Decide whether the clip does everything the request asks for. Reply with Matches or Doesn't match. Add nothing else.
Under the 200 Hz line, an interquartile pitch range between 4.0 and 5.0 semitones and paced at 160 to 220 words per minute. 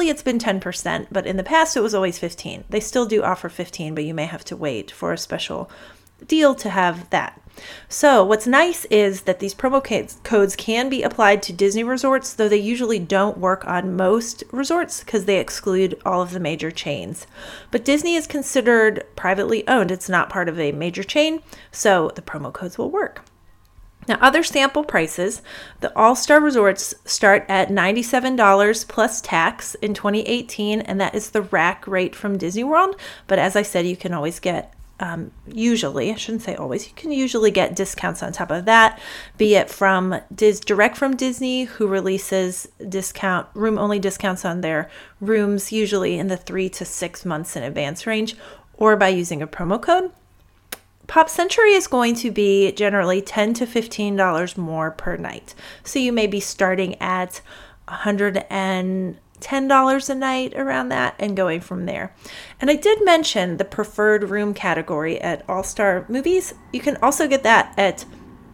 Doesn't match